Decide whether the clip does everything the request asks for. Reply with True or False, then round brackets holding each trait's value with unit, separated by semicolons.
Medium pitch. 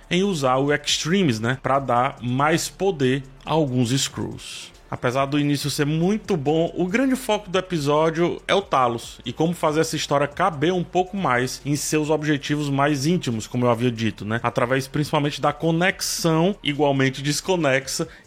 True (145 Hz)